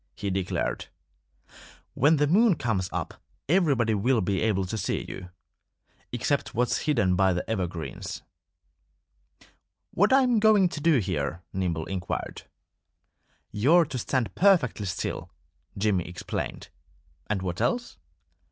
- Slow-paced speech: Yes, slow, 125 wpm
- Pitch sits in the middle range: No, low, 110 Hz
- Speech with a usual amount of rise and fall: No, wide, 8.9 semitones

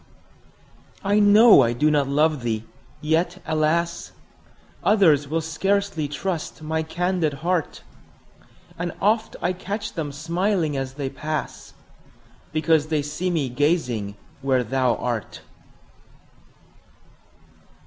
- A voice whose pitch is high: No, medium, 155 Hz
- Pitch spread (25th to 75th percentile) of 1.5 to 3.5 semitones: No, average, 4.0 semitones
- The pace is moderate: No, slow, 110 wpm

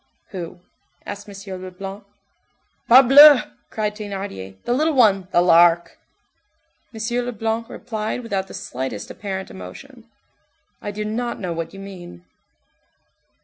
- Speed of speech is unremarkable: No, slow, 120 wpm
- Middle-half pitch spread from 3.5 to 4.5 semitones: Yes, average, 4.1 semitones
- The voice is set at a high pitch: Yes, high, 200 Hz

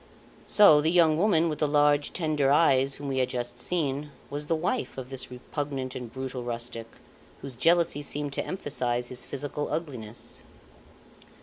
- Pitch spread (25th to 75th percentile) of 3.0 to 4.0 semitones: Yes, average, 3.4 semitones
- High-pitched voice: No, medium, 145 Hz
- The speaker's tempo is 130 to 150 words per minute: No, average, 165 wpm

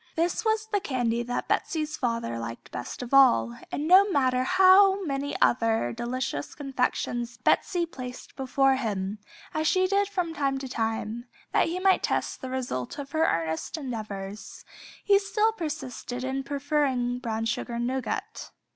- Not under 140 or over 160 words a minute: Yes, average, 155 wpm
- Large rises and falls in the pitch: Yes, wide, 5.7 semitones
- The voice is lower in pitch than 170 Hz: No, very high, 265 Hz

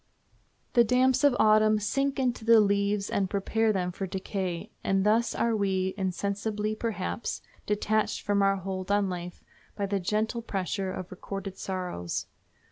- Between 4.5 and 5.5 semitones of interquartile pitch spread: No, narrow, 2.4 semitones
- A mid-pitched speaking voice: No, high, 200 Hz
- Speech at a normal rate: Yes, average, 150 wpm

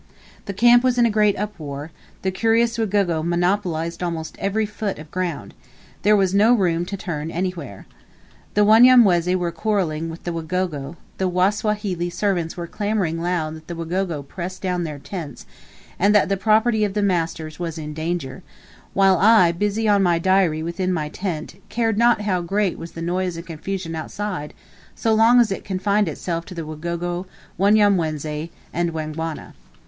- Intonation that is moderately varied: Yes, average, 3.8 semitones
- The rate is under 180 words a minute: Yes, average, 170 wpm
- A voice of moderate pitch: Yes, medium, 180 Hz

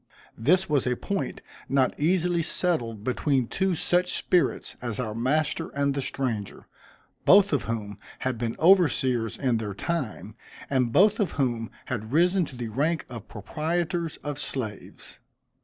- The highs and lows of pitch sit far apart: Yes, wide, 6.6 semitones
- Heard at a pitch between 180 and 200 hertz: No, medium, 140 Hz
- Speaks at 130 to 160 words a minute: Yes, average, 150 wpm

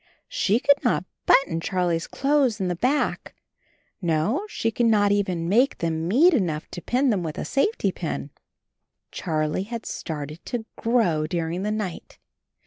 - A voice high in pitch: Yes, high, 195 Hz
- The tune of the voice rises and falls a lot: Yes, wide, 6.5 semitones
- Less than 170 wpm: Yes, average, 155 wpm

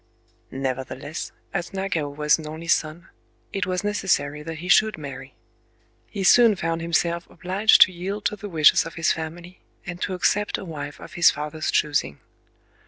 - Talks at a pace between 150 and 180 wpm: Yes, average, 170 wpm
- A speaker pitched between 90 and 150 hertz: No, medium, 170 Hz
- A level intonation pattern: No, average, 3.8 semitones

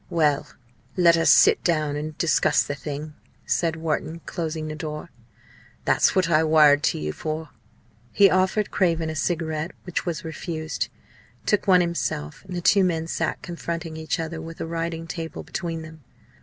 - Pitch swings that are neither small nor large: No, narrow, 1.6 semitones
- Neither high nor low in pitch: Yes, medium, 165 Hz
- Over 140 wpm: Yes, average, 170 wpm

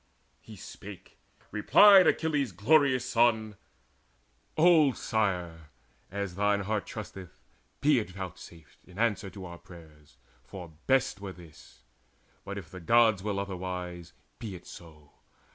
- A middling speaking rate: No, slow, 125 wpm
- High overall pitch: No, low, 100 Hz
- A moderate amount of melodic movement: Yes, average, 4.7 semitones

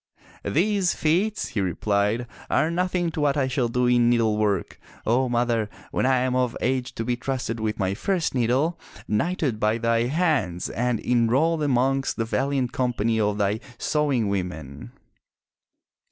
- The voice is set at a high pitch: No, low, 125 Hz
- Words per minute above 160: No, average, 155 wpm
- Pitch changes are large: No, average, 4.3 semitones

